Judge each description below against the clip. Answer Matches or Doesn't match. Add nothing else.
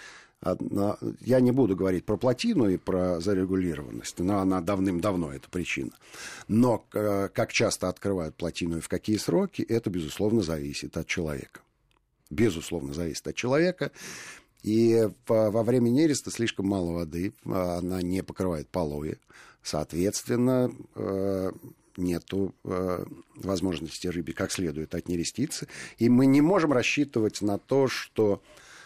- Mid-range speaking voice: Doesn't match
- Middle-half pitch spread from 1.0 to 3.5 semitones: Doesn't match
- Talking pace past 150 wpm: Doesn't match